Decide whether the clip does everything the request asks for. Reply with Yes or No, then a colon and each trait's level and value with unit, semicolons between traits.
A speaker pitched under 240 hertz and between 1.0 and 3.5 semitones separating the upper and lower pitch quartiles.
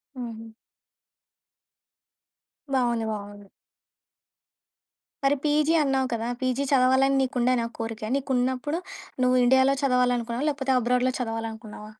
No: very high, 250 Hz; narrow, 2.6 semitones